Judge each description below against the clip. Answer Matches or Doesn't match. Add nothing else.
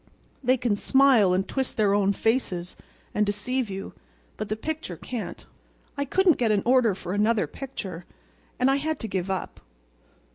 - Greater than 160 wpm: Matches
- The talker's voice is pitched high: Matches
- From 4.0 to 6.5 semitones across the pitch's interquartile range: Matches